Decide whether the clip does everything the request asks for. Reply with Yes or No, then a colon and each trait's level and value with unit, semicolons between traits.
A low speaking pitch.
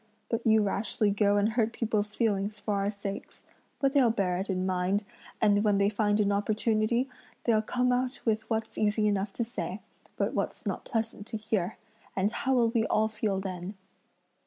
No: high, 215 Hz